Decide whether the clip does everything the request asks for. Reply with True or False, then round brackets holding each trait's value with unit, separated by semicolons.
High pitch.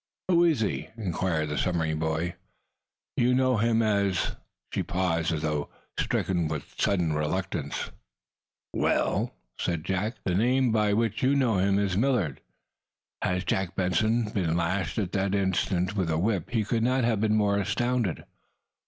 False (95 Hz)